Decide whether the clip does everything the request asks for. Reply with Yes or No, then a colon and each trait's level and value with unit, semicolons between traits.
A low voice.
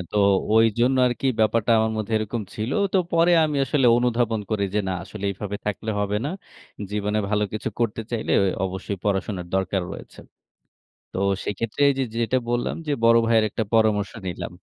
Yes: low, 110 Hz